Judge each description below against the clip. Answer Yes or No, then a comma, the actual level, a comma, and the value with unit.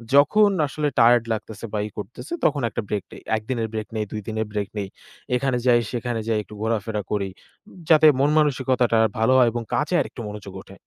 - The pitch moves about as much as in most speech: Yes, average, 3.9 semitones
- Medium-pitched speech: No, low, 115 Hz